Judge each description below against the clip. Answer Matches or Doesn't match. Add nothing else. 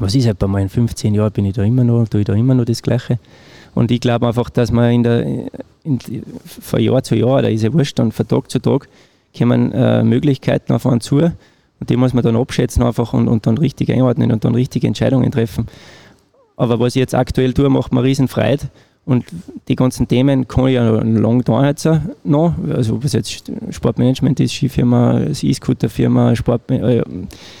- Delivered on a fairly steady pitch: Matches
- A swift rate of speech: Matches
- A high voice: Doesn't match